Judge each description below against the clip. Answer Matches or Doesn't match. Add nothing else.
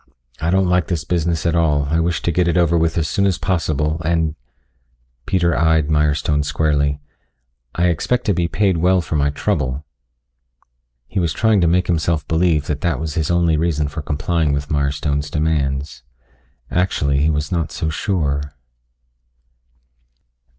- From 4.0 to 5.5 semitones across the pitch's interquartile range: Doesn't match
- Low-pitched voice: Matches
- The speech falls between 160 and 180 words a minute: Matches